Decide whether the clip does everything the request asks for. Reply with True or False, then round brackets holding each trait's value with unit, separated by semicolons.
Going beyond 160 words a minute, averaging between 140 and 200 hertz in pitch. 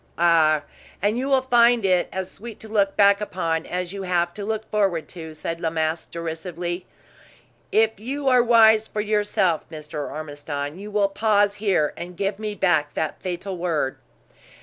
True (170 wpm; 185 Hz)